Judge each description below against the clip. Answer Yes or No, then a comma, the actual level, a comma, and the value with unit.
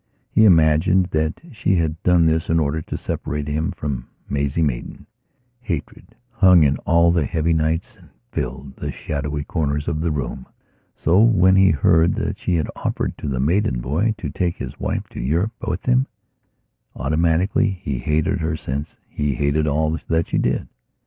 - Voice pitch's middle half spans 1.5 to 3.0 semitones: No, average, 3.4 semitones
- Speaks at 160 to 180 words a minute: Yes, average, 175 wpm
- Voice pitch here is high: No, very low, 80 Hz